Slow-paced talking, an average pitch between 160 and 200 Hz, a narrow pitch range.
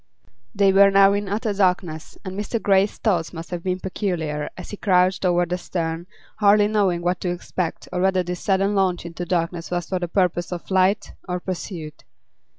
No: average, 190 wpm; medium, 185 Hz; narrow, 2.0 semitones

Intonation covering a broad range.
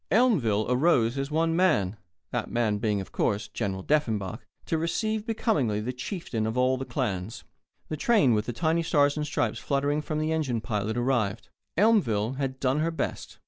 Yes: wide, 6.4 semitones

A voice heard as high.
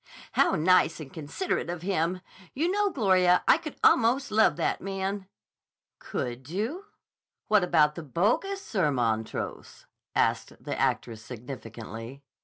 No: medium, 180 Hz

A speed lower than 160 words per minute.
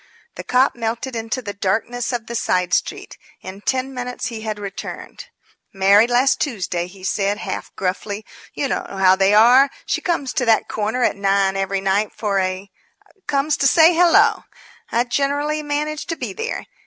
No: average, 175 wpm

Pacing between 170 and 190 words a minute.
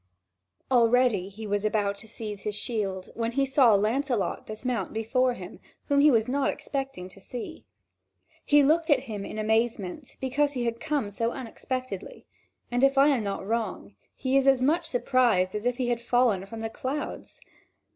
Yes: average, 175 wpm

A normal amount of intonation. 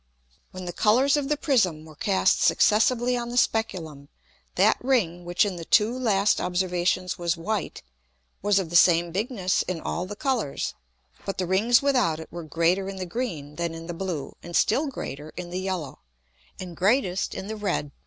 Yes: average, 4.5 semitones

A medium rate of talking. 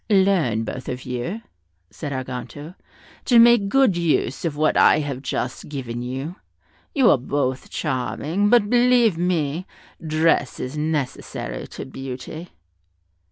No: slow, 130 wpm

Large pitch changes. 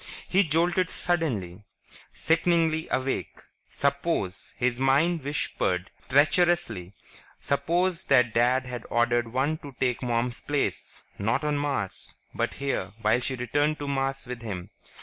No: average, 4.8 semitones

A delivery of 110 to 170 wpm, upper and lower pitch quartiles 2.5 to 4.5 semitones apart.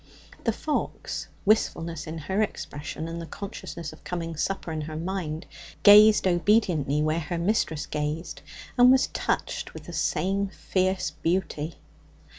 Yes: average, 140 wpm; average, 3.9 semitones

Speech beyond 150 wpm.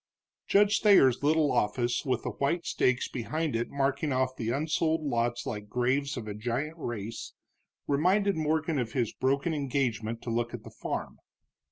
Yes: average, 165 wpm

